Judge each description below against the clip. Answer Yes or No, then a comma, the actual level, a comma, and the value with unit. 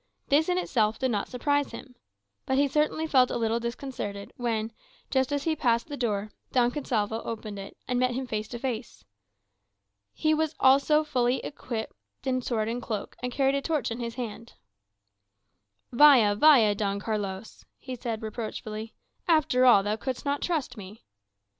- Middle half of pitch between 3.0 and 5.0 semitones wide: Yes, average, 3.8 semitones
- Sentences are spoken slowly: No, average, 170 wpm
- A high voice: Yes, high, 245 Hz